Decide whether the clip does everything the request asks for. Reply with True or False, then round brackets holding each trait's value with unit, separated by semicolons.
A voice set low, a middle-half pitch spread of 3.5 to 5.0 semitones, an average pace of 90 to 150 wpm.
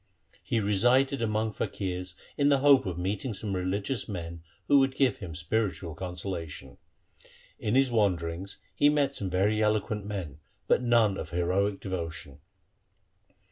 True (100 Hz; 4.6 semitones; 140 wpm)